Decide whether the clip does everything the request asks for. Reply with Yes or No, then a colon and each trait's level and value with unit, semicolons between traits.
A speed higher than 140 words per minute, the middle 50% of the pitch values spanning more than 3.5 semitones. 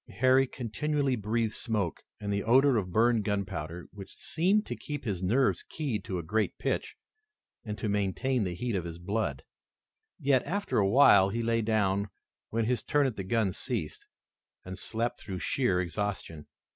Yes: average, 170 wpm; average, 4.6 semitones